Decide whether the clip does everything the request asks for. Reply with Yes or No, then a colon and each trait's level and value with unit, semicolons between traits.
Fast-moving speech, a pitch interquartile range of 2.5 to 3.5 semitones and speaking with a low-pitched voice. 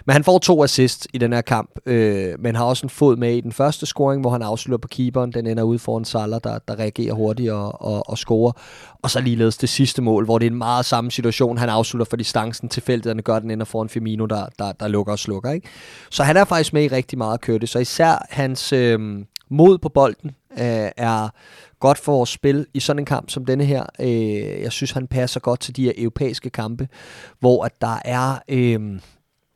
Yes: fast, 240 wpm; average, 2.9 semitones; low, 120 Hz